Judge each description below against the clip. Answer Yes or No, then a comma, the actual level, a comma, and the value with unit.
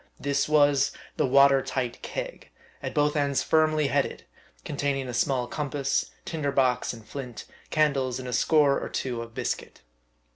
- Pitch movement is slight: Yes, narrow, 2.3 semitones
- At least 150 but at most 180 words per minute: Yes, average, 155 wpm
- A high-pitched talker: No, medium, 140 Hz